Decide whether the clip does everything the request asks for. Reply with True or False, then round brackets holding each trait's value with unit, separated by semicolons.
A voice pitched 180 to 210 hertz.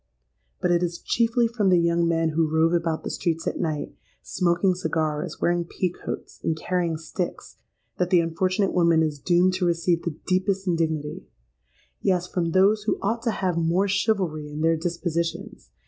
False (170 Hz)